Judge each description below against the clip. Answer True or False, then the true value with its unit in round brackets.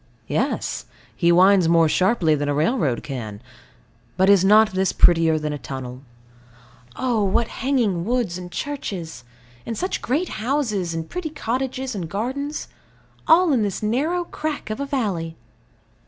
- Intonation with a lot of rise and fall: True (7.8 semitones)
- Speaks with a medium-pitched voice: False (200 Hz)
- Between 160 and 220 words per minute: False (150 wpm)